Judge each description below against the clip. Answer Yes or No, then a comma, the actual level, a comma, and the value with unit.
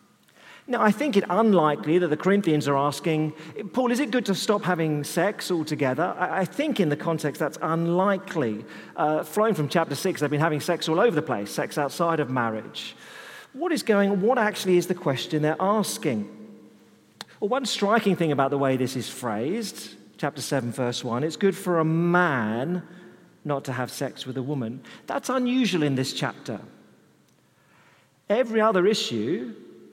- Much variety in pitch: Yes, wide, 5.8 semitones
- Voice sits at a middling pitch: Yes, medium, 165 Hz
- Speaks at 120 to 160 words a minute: No, average, 175 wpm